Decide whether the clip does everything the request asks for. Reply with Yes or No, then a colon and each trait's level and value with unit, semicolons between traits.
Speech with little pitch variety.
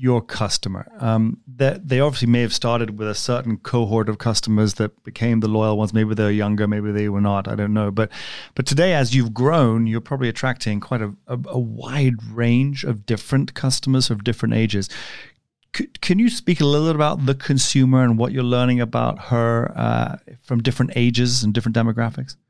No: average, 3.0 semitones